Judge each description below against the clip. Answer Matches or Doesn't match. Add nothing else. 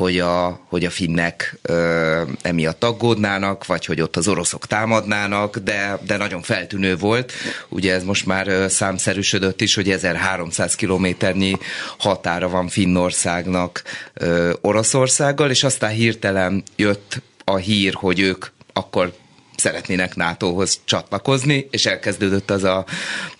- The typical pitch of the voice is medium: Doesn't match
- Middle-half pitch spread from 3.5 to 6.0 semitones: Doesn't match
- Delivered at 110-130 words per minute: Matches